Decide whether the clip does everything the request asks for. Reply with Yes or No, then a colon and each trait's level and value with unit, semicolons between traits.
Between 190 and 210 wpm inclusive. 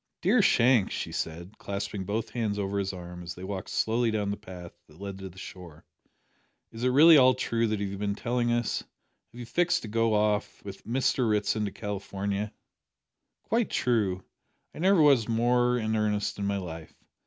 Yes: average, 195 wpm